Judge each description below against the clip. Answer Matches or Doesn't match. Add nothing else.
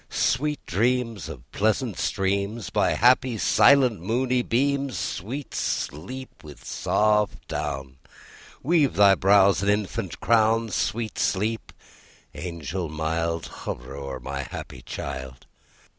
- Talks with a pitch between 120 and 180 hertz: Doesn't match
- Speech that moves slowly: Matches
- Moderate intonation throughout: Doesn't match